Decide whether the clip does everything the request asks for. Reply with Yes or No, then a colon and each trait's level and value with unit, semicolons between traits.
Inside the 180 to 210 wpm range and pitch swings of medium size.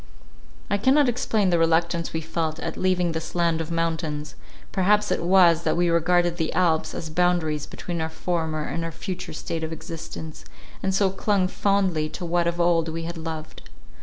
No: average, 185 wpm; narrow, 2.0 semitones